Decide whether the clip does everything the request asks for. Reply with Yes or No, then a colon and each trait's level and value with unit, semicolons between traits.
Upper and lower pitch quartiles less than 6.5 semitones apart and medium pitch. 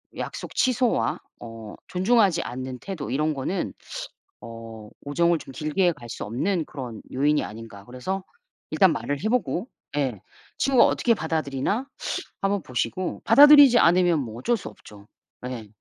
No: wide, 8.3 semitones; medium, 155 Hz